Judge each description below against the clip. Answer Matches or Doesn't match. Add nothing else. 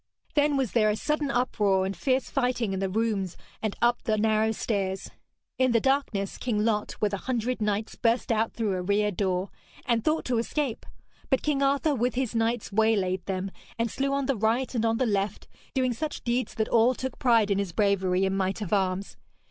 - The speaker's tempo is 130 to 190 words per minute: Doesn't match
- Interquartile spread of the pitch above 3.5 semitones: Matches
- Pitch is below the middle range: Doesn't match